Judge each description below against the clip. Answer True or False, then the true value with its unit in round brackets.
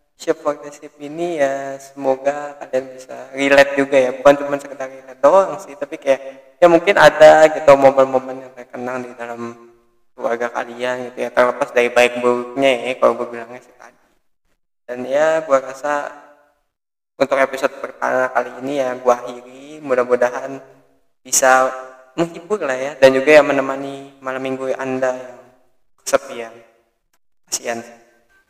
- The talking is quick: True (145 wpm)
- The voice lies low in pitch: True (130 Hz)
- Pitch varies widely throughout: False (2.4 semitones)